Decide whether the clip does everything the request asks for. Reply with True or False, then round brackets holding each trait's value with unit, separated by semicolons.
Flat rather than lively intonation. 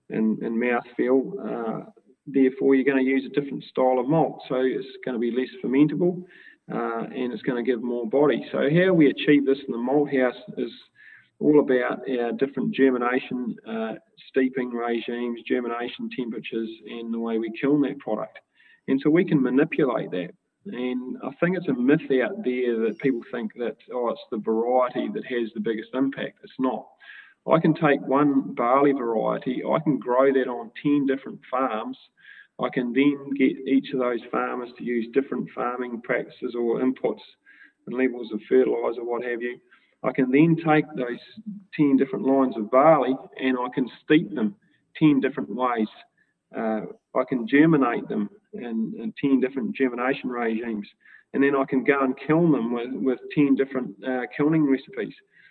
False (3.1 semitones)